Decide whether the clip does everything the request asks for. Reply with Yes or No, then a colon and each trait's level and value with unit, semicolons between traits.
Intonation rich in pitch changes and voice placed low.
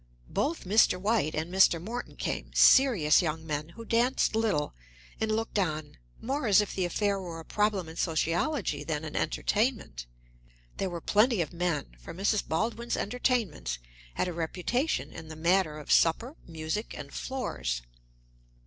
No: wide, 5.9 semitones; medium, 185 Hz